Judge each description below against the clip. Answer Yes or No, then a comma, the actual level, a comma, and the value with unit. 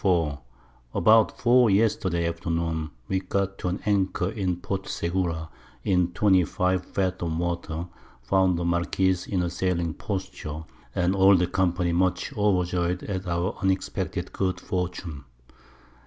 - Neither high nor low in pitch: No, very low, 90 Hz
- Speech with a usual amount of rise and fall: No, narrow, 1.8 semitones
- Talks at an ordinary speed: No, slow, 130 wpm